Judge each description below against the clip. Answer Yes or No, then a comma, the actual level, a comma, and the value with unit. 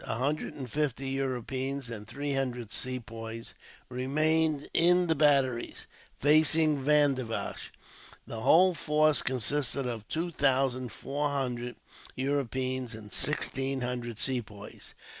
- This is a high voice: No, low, 135 Hz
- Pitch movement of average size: Yes, average, 3.1 semitones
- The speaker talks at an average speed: No, slow, 115 wpm